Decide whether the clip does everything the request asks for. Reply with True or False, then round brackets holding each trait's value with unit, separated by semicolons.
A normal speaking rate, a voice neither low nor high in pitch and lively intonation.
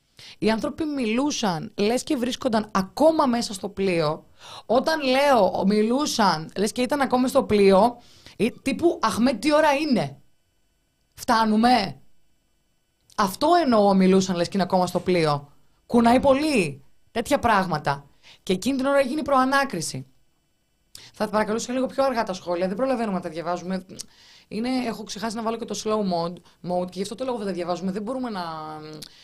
False (160 wpm; 215 Hz; 6.3 semitones)